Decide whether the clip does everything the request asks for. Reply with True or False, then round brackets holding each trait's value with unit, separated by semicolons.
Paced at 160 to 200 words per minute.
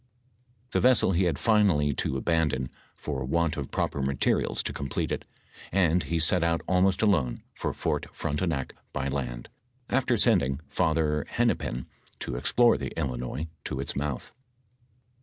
False (150 wpm)